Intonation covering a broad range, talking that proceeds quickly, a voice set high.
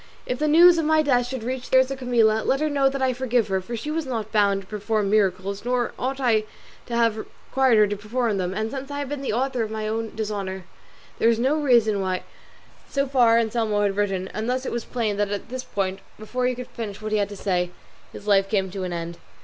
No: average, 4.0 semitones; fast, 255 wpm; high, 225 Hz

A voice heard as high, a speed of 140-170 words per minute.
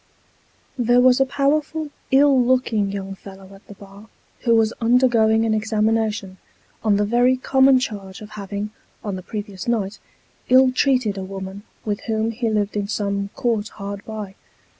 Yes: high, 220 Hz; average, 160 wpm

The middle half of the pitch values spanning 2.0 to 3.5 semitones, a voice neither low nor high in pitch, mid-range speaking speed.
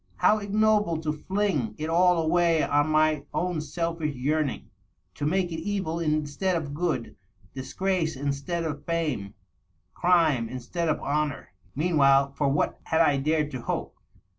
Yes: average, 3.2 semitones; medium, 155 Hz; average, 160 wpm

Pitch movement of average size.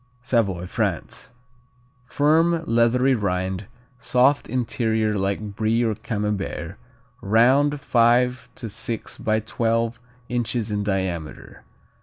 Yes: average, 3.3 semitones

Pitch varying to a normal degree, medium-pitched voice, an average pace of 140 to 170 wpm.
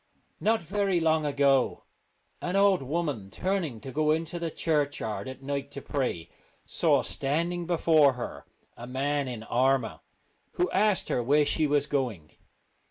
Yes: average, 4.4 semitones; medium, 145 Hz; average, 150 wpm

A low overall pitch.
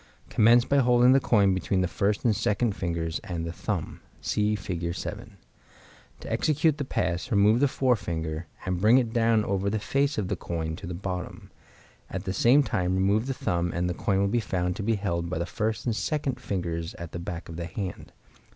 Yes: low, 100 Hz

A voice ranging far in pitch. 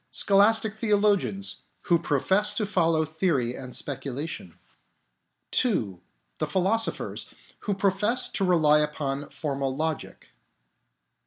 Yes: wide, 6.1 semitones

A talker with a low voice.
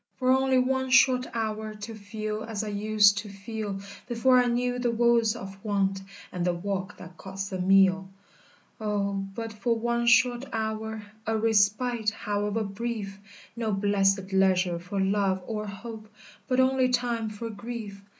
No: high, 215 Hz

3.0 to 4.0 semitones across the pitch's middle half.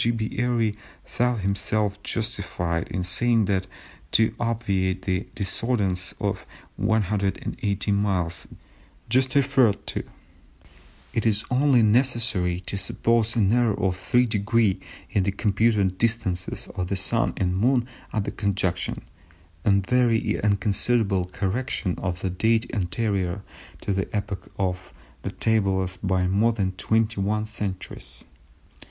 Yes: average, 3.3 semitones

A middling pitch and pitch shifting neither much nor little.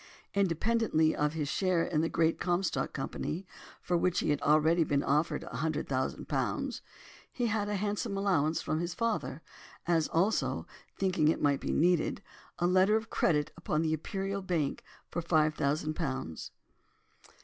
Yes: medium, 165 Hz; average, 3.8 semitones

